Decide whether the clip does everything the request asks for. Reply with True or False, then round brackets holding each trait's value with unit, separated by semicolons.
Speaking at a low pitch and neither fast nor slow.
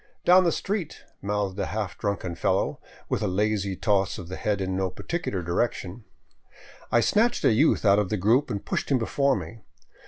True (105 Hz; 190 wpm)